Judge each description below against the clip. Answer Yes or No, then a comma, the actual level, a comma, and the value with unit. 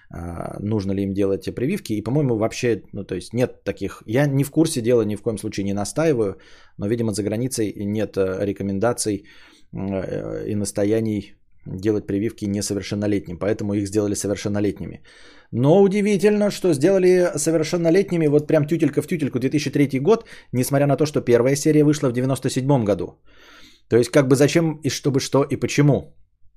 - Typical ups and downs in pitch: No, wide, 6.2 semitones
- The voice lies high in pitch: No, low, 120 Hz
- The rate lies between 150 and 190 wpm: Yes, average, 160 wpm